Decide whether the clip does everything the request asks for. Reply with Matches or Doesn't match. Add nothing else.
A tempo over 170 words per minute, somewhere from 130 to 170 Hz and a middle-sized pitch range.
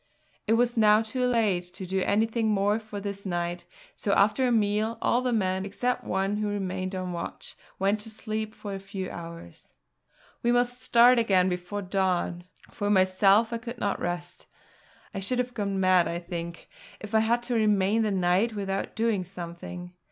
Doesn't match